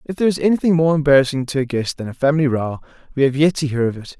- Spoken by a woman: No, male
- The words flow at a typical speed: No, fast, 285 wpm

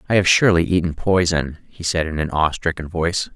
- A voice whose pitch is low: Yes, very low, 85 Hz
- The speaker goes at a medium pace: No, fast, 215 wpm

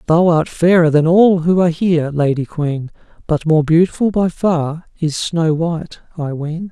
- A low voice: No, medium, 165 Hz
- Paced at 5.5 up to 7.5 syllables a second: No, 4.6 syllables/s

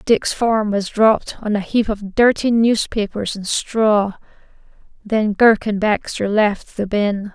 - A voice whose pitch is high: Yes, high, 210 Hz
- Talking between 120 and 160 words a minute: Yes, average, 155 wpm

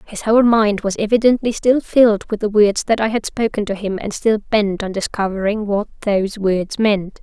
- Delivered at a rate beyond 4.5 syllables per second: Yes, 5.0 syllables/s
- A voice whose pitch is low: No, high, 210 Hz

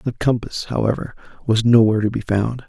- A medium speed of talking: Yes, average, 180 wpm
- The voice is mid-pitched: No, low, 115 Hz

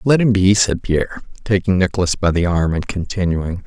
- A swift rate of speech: No, average, 195 wpm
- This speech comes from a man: Yes, male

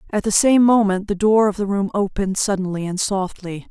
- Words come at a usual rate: No, fast, 210 wpm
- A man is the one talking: No, female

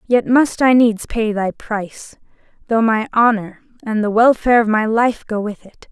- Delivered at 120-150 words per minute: No, average, 195 wpm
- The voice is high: Yes, high, 225 Hz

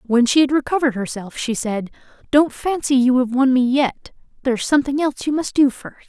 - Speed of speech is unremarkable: No, fast, 215 wpm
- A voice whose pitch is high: Yes, very high, 265 Hz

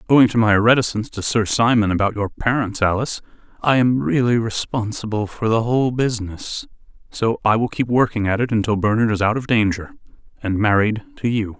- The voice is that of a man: Yes, male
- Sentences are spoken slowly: No, average, 185 wpm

